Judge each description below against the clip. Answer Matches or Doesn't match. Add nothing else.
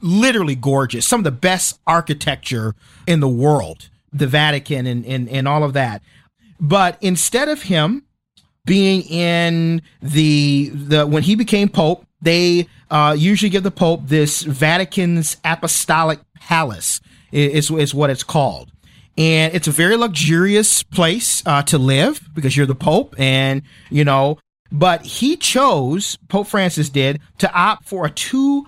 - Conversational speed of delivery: Matches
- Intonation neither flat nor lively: Matches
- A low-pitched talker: Doesn't match